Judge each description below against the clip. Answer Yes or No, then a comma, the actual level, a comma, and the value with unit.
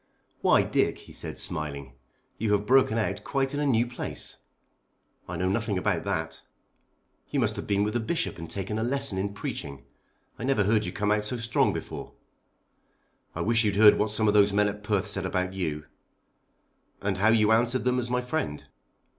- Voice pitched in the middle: No, low, 105 Hz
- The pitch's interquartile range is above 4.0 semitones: No, average, 3.4 semitones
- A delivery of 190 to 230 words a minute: Yes, average, 195 wpm